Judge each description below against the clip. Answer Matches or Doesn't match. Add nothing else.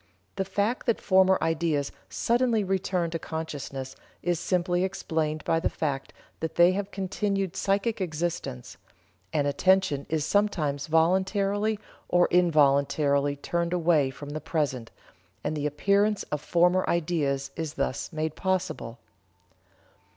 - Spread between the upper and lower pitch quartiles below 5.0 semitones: Matches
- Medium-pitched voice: Matches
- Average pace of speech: Doesn't match